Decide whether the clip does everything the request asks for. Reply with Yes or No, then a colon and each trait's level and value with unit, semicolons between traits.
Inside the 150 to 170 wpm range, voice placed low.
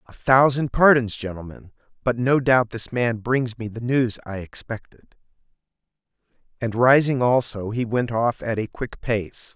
Yes: average, 155 wpm; low, 120 Hz